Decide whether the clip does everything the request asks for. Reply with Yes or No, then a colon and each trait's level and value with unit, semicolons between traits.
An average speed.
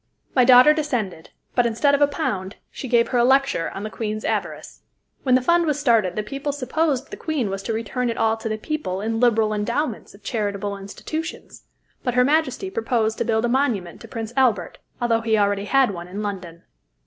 No: fast, 210 wpm